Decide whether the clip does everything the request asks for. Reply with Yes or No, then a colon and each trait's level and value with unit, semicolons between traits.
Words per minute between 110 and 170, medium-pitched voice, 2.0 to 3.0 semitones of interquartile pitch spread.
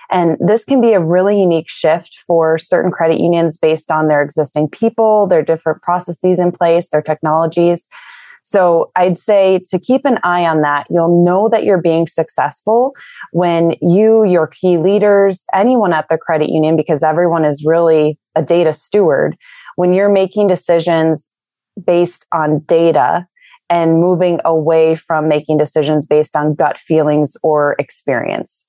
Yes: average, 155 wpm; medium, 170 Hz; average, 2.7 semitones